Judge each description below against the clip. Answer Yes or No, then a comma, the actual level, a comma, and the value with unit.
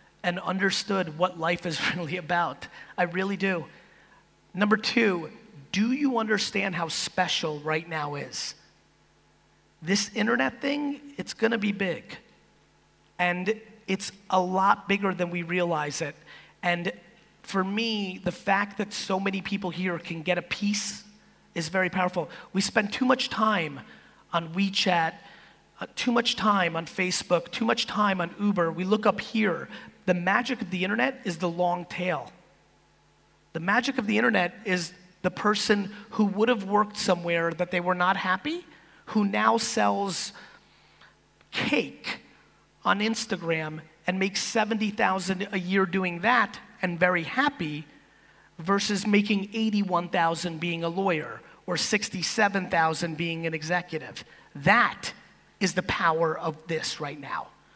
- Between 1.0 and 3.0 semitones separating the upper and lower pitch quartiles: No, average, 3.4 semitones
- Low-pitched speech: No, high, 190 Hz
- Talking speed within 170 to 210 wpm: No, average, 140 wpm